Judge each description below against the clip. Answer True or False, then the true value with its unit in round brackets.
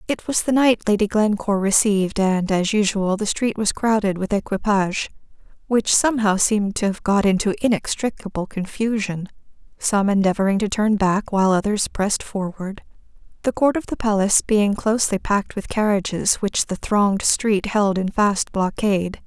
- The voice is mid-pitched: False (205 Hz)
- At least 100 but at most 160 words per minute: True (155 wpm)